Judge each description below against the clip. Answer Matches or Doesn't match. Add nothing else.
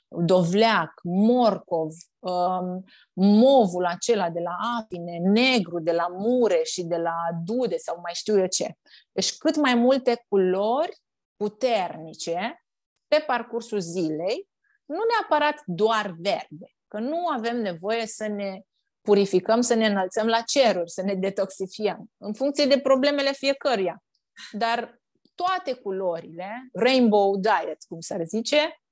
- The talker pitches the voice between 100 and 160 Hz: Doesn't match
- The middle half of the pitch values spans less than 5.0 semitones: Doesn't match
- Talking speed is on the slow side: Doesn't match